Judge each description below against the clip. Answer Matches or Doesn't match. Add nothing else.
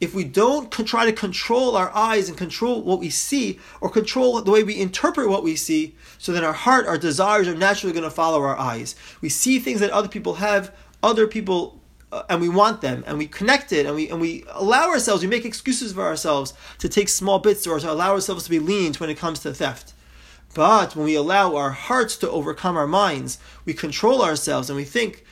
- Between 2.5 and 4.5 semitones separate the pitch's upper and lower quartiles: Doesn't match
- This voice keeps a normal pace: Doesn't match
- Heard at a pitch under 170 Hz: Doesn't match